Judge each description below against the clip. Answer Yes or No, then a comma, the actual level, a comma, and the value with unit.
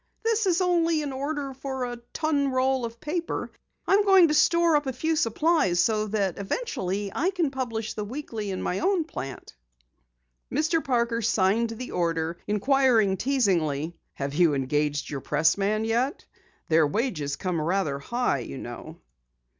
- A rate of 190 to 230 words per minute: No, average, 155 wpm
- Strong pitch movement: Yes, wide, 8.5 semitones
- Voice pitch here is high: Yes, high, 235 Hz